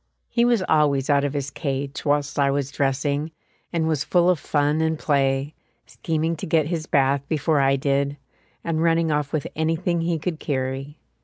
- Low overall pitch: No, medium, 150 Hz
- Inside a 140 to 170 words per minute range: No, average, 180 wpm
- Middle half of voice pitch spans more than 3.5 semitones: No, narrow, 2.5 semitones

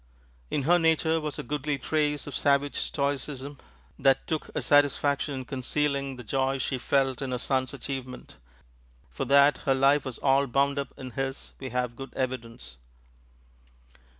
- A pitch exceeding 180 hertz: No, low, 135 Hz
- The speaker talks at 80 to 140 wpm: No, average, 160 wpm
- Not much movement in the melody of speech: Yes, narrow, 1.7 semitones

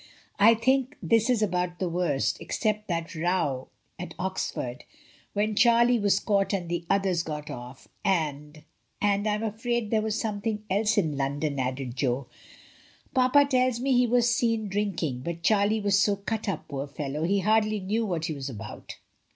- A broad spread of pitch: Yes, wide, 5.7 semitones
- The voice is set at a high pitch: Yes, high, 200 Hz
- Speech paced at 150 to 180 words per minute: Yes, average, 175 wpm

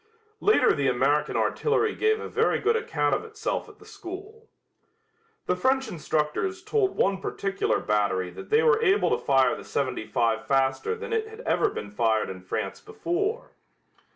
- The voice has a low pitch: No, very high, 260 Hz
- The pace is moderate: Yes, average, 170 wpm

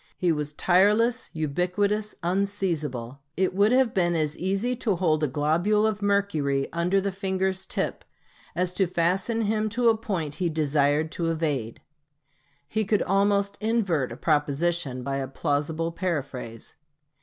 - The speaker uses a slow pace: No, average, 145 wpm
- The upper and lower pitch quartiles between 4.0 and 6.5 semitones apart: Yes, average, 5.1 semitones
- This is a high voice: No, medium, 180 Hz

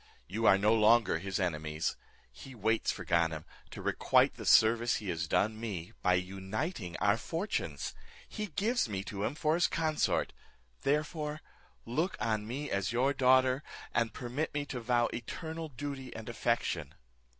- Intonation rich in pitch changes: Yes, wide, 6.6 semitones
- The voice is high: No, low, 115 Hz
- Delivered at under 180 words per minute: Yes, average, 160 wpm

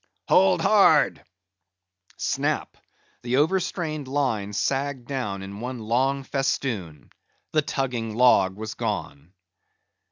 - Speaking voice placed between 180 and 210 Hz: No, low, 125 Hz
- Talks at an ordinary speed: No, slow, 100 wpm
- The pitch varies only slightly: No, average, 5.2 semitones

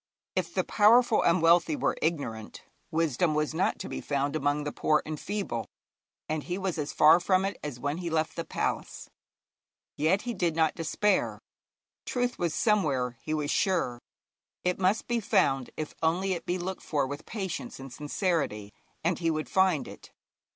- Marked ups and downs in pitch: No, average, 4.2 semitones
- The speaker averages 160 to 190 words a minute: Yes, average, 180 wpm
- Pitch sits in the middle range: Yes, medium, 165 Hz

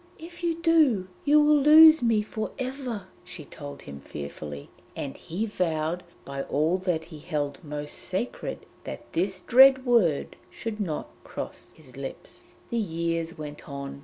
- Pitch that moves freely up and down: Yes, wide, 9.0 semitones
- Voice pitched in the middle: Yes, medium, 180 Hz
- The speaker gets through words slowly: No, average, 155 wpm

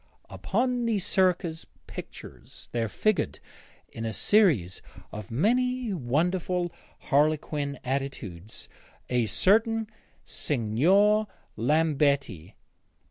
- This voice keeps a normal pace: No, slow, 80 wpm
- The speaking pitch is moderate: Yes, medium, 155 Hz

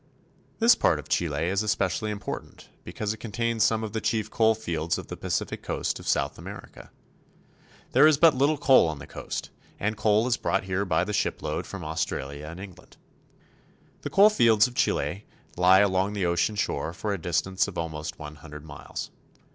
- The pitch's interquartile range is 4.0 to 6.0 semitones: Yes, average, 4.9 semitones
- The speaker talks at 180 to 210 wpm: Yes, average, 185 wpm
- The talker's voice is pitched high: No, low, 100 Hz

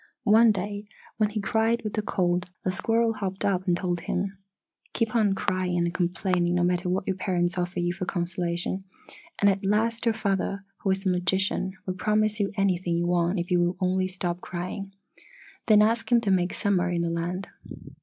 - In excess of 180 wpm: Yes, average, 195 wpm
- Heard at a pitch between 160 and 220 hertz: Yes, medium, 185 Hz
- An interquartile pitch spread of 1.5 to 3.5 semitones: Yes, narrow, 2.6 semitones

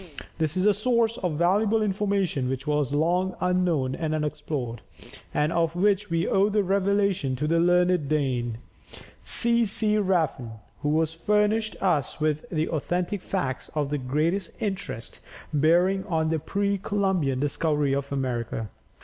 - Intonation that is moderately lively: Yes, average, 5.0 semitones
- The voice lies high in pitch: No, medium, 165 Hz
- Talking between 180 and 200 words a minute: No, average, 145 wpm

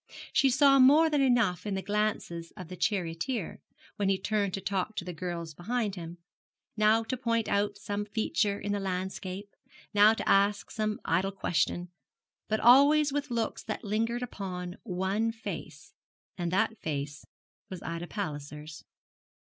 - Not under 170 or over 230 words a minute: No, average, 155 wpm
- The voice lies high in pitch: Yes, high, 205 Hz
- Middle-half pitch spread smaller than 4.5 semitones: Yes, average, 3.9 semitones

